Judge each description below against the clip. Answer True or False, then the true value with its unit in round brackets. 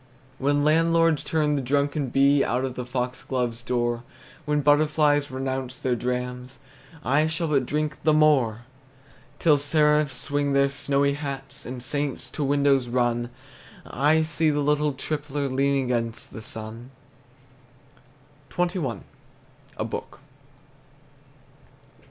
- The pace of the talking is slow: True (120 wpm)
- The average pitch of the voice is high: False (140 Hz)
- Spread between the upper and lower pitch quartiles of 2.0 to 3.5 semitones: True (3.0 semitones)